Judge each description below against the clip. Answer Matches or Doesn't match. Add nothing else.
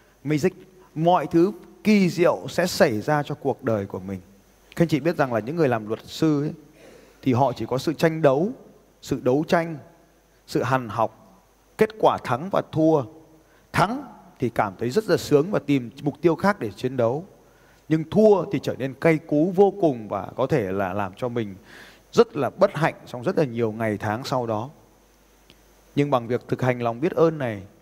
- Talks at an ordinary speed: Matches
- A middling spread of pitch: Doesn't match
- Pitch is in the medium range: Matches